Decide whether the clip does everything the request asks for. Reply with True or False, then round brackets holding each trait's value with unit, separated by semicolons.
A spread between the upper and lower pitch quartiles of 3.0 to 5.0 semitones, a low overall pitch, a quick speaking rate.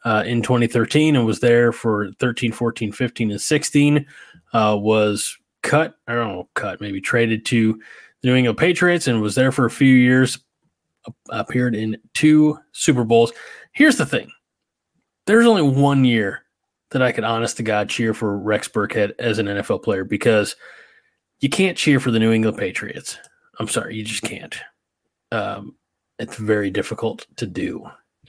False (3.6 semitones; 120 Hz; 170 wpm)